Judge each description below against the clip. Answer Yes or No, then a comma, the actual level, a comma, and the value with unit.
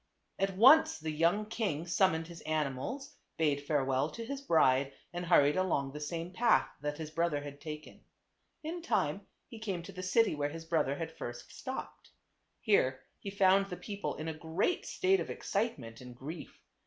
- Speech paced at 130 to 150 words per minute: No, average, 180 wpm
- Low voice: No, medium, 165 Hz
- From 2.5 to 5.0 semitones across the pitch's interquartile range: No, wide, 5.4 semitones